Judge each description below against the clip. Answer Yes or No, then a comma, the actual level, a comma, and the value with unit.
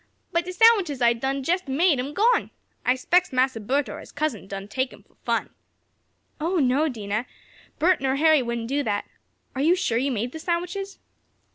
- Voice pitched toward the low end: No, very high, 275 Hz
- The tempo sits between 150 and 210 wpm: Yes, average, 190 wpm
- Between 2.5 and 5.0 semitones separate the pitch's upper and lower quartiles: No, wide, 5.6 semitones